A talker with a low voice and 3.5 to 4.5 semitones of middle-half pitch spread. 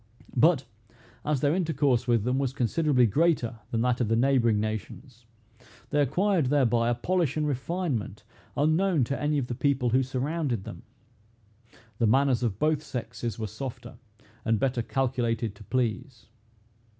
Yes: low, 130 Hz; average, 3.9 semitones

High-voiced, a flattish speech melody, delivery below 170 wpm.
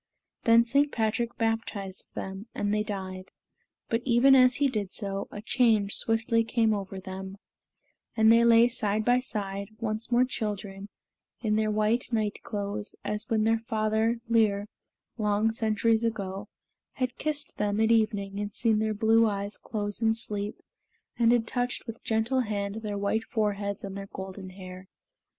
Yes: high, 215 Hz; narrow, 2.2 semitones; average, 160 wpm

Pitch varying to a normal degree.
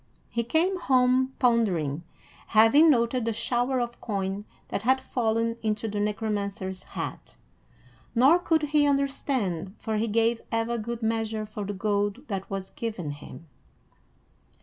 Yes: average, 3.6 semitones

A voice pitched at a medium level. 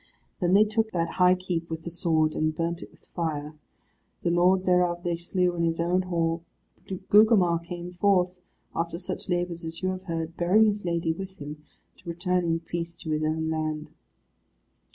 Yes: medium, 170 Hz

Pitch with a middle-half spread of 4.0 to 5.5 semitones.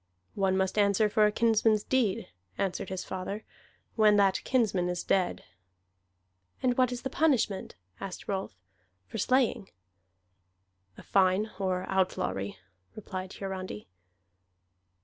No: narrow, 2.6 semitones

